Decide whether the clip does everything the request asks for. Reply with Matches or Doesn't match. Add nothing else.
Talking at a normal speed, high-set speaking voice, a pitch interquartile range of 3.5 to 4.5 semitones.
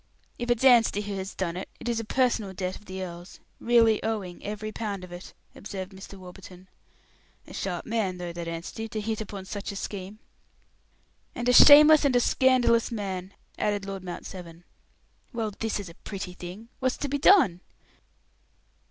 Matches